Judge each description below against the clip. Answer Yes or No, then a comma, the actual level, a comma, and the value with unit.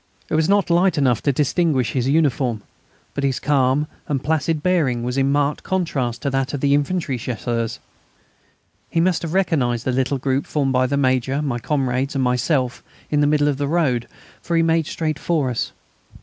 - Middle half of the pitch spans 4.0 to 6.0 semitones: No, average, 3.5 semitones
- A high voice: No, medium, 140 Hz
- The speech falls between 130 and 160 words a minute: No, average, 190 wpm